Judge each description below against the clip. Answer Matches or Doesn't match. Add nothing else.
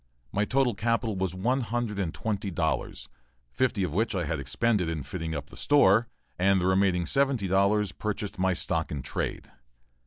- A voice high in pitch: Doesn't match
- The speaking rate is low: Doesn't match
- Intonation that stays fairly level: Doesn't match